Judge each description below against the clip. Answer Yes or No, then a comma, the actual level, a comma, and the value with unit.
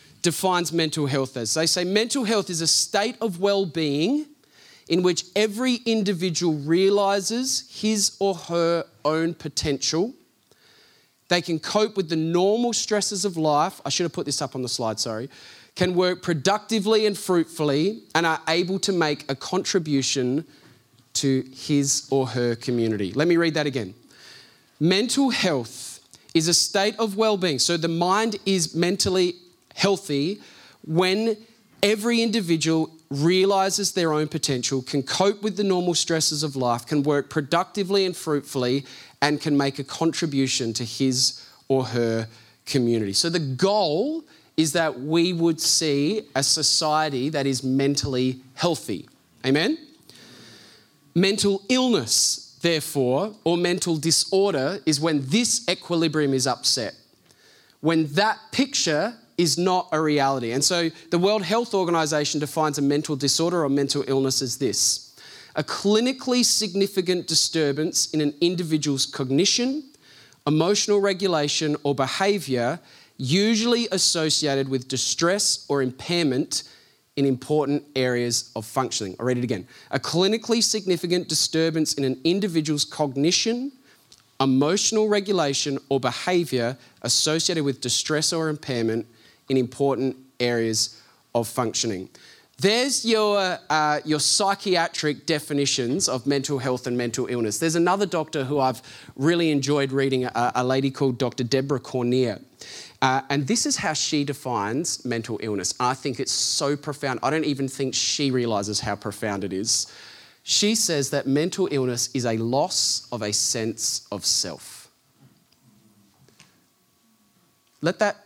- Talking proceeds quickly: No, average, 140 wpm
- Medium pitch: Yes, medium, 155 Hz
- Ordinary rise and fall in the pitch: No, wide, 5.7 semitones